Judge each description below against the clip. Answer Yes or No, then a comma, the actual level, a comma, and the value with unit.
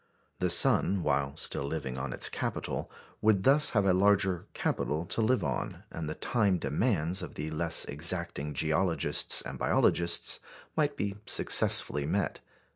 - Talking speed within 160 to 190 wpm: No, average, 150 wpm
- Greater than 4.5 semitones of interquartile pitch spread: Yes, average, 4.9 semitones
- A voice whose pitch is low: Yes, very low, 85 Hz